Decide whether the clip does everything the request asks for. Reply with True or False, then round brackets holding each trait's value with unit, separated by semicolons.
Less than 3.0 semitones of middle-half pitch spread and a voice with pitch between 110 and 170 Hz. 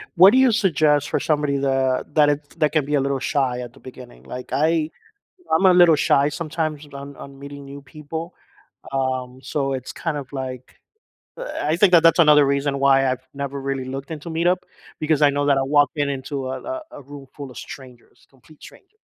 True (2.5 semitones; 140 Hz)